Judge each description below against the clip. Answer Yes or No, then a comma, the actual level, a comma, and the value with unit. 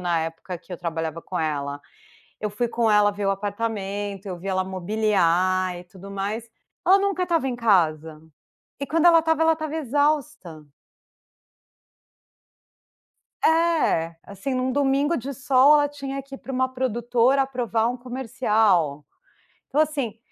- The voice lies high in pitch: Yes, high, 225 Hz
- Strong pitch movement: Yes, wide, 6.7 semitones